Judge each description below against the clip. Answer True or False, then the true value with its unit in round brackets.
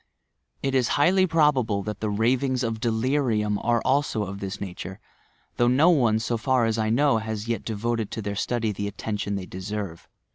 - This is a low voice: True (115 Hz)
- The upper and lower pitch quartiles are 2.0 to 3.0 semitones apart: False (3.7 semitones)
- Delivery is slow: False (195 wpm)